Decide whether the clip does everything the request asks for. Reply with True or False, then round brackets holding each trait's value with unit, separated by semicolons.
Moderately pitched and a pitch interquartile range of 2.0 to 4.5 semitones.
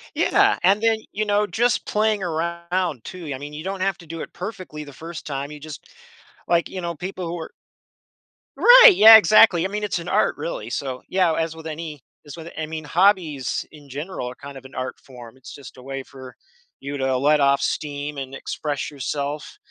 False (160 Hz; 4.9 semitones)